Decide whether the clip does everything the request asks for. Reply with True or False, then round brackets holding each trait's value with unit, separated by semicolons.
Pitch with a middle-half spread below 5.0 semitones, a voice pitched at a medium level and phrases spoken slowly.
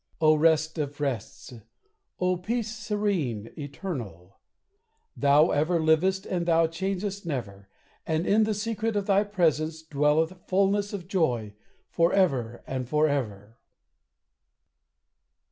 False (5.4 semitones; 160 Hz; 110 wpm)